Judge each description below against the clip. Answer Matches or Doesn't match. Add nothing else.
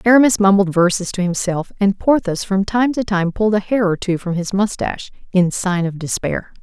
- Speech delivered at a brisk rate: Matches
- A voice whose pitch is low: Doesn't match